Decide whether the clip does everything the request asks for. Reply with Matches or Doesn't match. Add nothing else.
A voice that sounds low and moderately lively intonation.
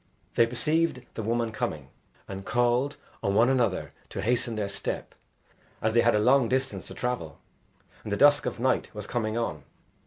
Matches